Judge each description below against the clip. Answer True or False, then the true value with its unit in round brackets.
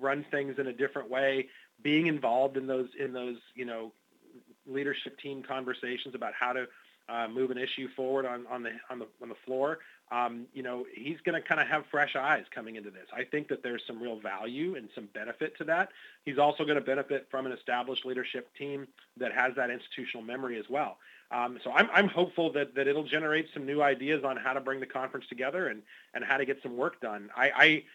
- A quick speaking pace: True (225 wpm)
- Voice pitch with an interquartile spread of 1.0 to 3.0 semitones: True (2.4 semitones)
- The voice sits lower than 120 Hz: False (135 Hz)